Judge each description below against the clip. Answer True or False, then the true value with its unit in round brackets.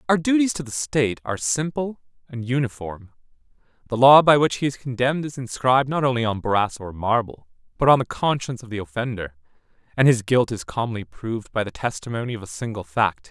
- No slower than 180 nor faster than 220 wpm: True (200 wpm)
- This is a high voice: False (120 Hz)